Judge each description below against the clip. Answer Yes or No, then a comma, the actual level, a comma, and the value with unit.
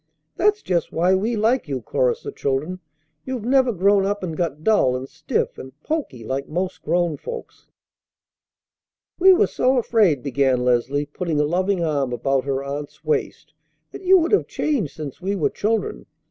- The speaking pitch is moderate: Yes, medium, 175 Hz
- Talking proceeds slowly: No, average, 175 wpm